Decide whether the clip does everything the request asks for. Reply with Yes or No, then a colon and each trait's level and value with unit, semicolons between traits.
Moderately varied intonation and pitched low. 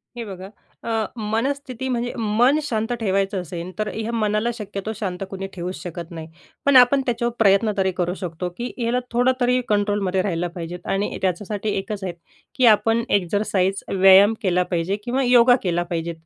No: average, 4.1 semitones; high, 205 Hz